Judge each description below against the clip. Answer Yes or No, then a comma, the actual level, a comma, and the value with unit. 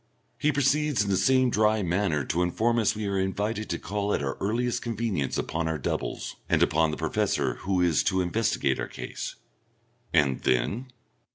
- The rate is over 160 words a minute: Yes, average, 180 wpm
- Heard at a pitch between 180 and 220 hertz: No, low, 100 Hz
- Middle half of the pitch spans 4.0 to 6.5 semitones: Yes, average, 5.3 semitones